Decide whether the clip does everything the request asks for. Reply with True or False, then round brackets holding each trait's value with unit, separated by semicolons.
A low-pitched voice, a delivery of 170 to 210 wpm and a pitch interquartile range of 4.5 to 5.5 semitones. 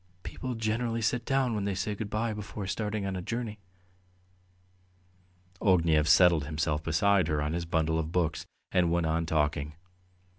False (90 Hz; 160 wpm; 5.1 semitones)